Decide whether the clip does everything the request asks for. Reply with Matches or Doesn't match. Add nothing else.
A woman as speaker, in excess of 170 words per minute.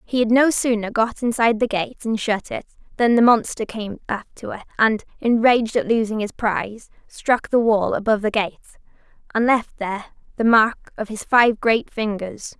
Matches